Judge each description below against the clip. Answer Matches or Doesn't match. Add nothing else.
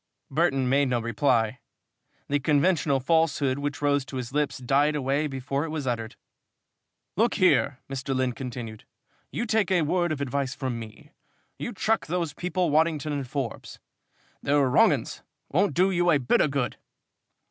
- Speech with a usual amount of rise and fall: Matches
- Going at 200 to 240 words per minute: Doesn't match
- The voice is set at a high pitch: Doesn't match